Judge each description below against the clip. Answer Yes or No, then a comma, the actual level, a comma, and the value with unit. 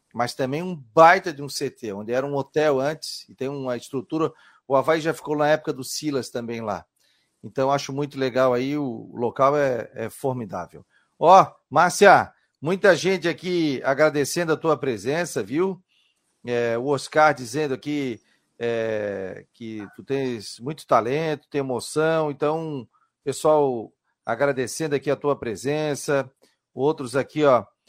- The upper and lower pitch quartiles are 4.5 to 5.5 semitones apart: No, average, 3.7 semitones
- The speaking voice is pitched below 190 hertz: Yes, medium, 140 Hz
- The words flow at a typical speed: Yes, average, 150 wpm